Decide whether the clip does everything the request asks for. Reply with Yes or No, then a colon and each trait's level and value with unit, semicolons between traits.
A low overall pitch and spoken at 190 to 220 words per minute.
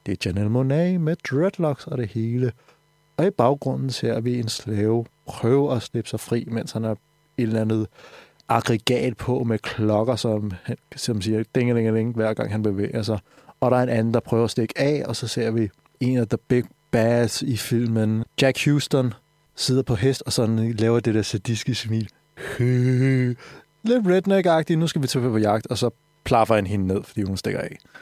Yes: low, 120 Hz; average, 200 wpm